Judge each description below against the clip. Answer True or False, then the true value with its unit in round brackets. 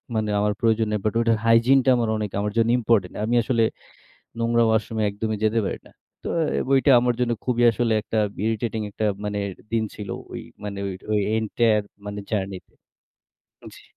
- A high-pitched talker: False (110 Hz)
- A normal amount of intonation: False (1.8 semitones)